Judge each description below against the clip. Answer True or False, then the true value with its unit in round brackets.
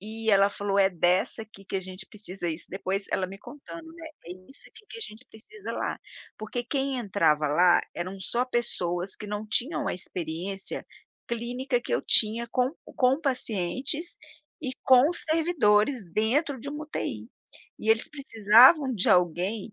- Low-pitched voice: False (220 Hz)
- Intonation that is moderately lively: False (5.7 semitones)